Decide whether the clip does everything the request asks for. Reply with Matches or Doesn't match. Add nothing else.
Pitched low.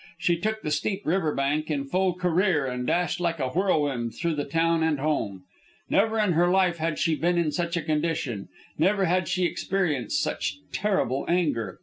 Doesn't match